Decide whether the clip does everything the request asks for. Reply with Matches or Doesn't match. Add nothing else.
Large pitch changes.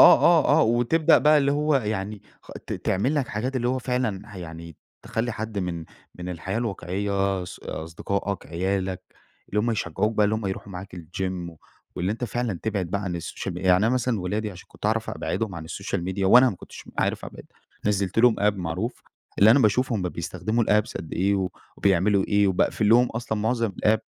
Doesn't match